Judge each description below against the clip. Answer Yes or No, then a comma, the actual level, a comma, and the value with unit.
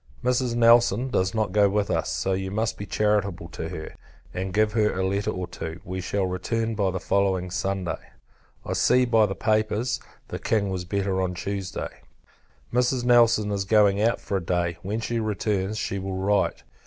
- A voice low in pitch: Yes, low, 100 Hz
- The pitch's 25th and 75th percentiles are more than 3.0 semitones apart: No, average, 2.7 semitones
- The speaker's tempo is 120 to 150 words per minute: No, average, 190 wpm